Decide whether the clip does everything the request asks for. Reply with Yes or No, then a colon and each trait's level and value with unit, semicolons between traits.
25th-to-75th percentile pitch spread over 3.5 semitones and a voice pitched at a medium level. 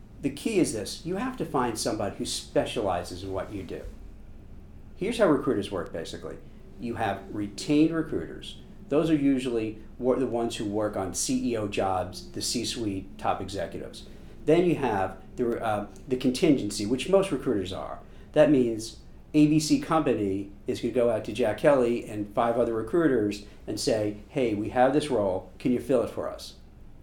No: average, 4.5 semitones; low, 115 Hz